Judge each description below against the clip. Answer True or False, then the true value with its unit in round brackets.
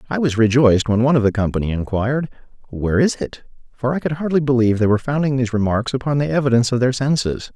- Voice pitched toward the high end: False (125 Hz)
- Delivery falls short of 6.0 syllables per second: False (7.2 syllables/s)